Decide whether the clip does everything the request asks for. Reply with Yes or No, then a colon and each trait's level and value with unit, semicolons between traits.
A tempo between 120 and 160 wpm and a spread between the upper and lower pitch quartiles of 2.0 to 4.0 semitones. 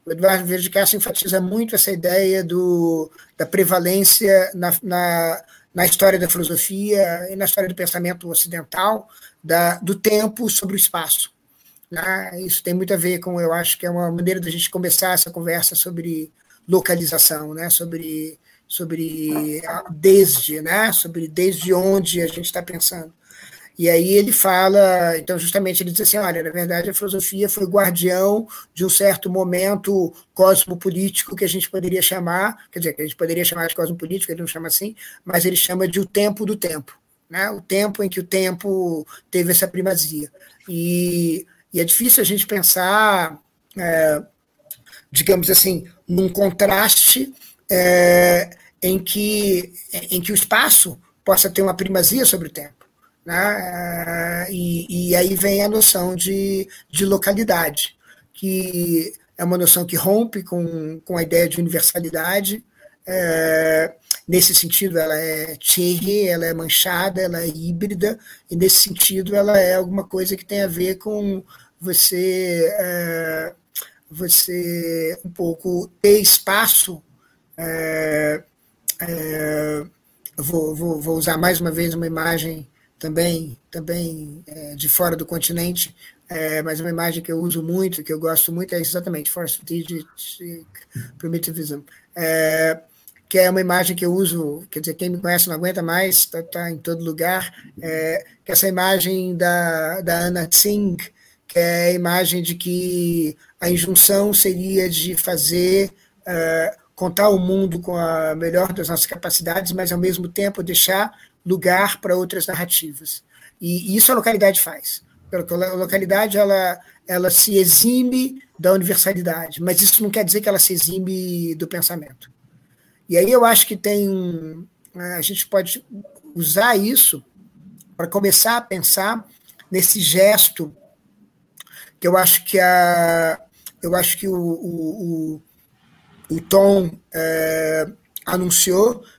Yes: average, 150 wpm; narrow, 2.5 semitones